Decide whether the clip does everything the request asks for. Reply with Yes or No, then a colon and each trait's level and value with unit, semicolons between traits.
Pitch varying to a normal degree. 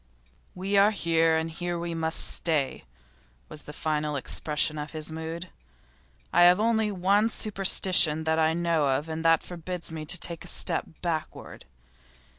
No: narrow, 2.3 semitones